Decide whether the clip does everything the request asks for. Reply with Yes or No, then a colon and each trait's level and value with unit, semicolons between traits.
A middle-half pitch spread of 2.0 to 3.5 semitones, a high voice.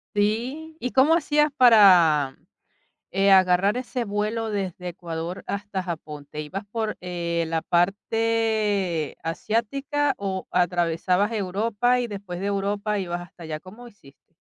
No: average, 4.3 semitones; high, 200 Hz